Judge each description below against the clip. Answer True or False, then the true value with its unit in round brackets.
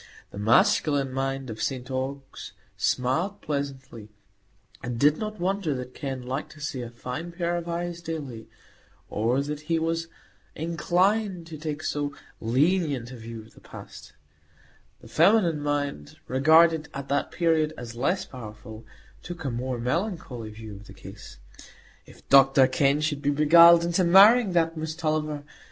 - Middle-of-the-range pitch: True (145 Hz)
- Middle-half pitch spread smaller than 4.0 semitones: False (4.7 semitones)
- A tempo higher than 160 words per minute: False (155 wpm)